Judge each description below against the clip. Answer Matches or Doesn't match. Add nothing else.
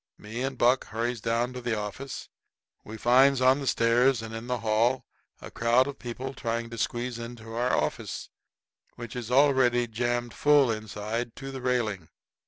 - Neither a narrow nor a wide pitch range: Doesn't match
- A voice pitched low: Matches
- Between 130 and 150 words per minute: Doesn't match